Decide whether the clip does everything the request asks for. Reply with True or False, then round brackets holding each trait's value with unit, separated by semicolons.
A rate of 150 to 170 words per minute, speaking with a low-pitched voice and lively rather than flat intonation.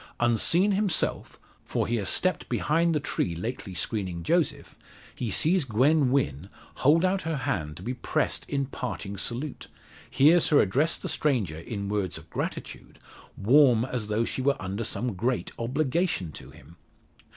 True (160 wpm; 125 Hz; 6.9 semitones)